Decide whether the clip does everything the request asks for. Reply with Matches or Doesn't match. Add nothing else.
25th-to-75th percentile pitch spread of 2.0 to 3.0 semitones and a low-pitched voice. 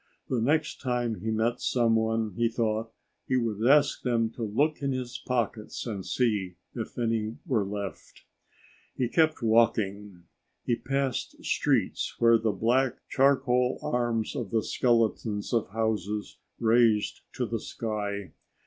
Matches